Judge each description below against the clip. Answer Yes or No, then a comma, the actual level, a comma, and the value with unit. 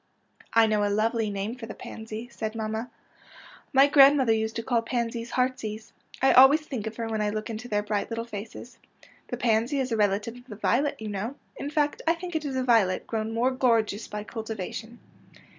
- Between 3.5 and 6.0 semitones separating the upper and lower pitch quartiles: No, average, 2.7 semitones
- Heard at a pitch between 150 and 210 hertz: No, high, 230 Hz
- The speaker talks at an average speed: No, fast, 215 wpm